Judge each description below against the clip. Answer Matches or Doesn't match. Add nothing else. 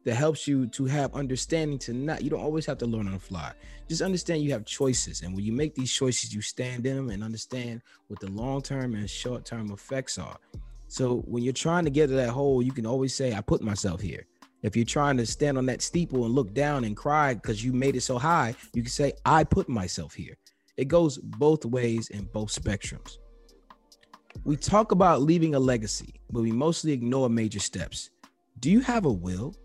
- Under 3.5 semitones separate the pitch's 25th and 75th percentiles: Doesn't match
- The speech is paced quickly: Matches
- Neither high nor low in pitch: Doesn't match